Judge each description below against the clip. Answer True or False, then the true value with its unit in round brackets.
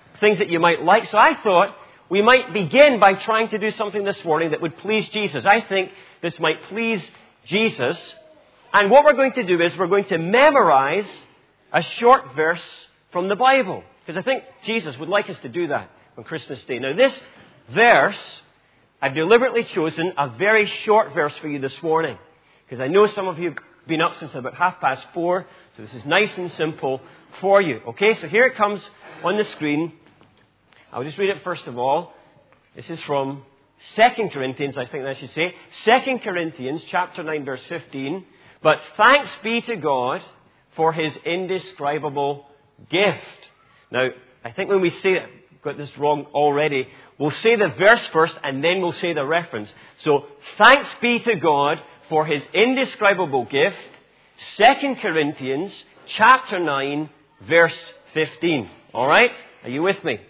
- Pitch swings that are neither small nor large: False (5.9 semitones)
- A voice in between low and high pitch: True (175 Hz)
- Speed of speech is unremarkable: True (175 wpm)